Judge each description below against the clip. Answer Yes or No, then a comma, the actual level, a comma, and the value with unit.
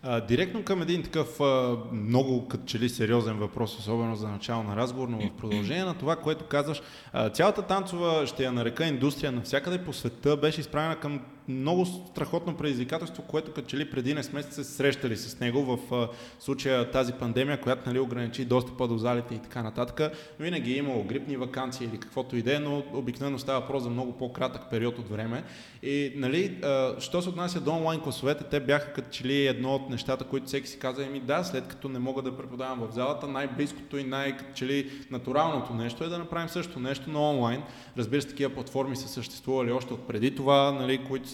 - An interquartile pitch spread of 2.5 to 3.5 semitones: Yes, average, 2.8 semitones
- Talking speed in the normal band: No, fast, 200 wpm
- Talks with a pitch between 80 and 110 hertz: No, low, 135 Hz